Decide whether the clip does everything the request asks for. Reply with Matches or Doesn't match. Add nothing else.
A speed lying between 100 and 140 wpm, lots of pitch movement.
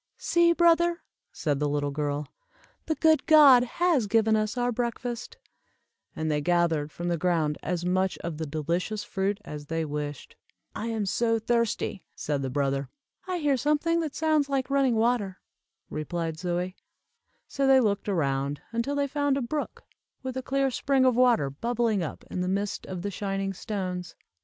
Doesn't match